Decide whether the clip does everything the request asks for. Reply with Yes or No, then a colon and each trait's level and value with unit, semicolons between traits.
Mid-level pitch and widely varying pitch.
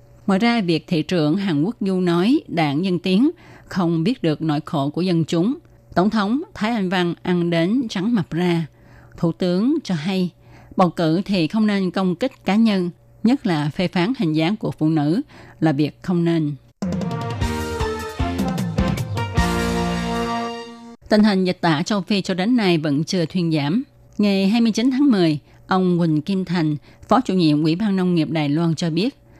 No: medium, 175 Hz; average, 4.5 semitones